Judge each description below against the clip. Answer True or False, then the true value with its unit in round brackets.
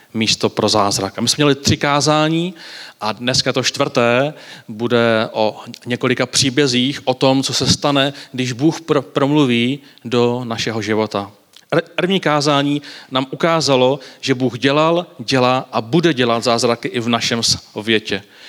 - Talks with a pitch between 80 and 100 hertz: False (130 Hz)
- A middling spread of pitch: True (3.6 semitones)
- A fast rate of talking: False (150 wpm)